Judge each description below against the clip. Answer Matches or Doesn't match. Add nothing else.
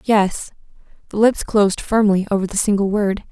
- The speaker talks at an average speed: Matches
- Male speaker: Doesn't match